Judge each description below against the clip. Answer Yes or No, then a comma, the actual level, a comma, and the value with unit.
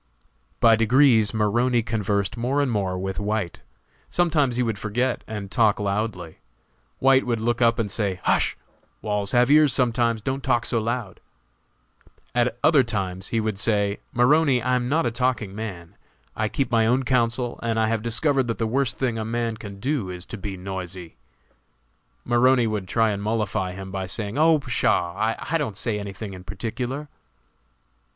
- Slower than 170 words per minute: No, average, 175 wpm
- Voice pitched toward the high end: No, low, 115 Hz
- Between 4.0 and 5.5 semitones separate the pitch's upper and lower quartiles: No, average, 3.5 semitones